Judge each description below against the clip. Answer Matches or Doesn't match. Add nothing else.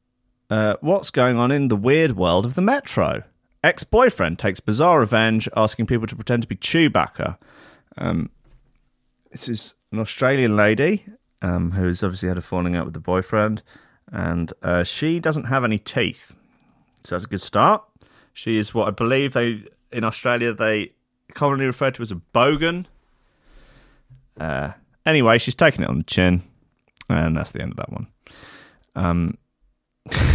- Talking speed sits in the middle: Matches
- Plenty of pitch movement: Matches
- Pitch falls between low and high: Doesn't match